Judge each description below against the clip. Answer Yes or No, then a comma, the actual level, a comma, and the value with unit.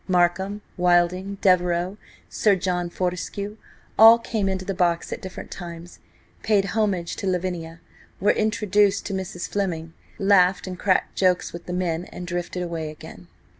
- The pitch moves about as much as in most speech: No, narrow, 2.2 semitones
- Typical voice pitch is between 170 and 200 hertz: Yes, medium, 185 Hz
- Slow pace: No, average, 145 wpm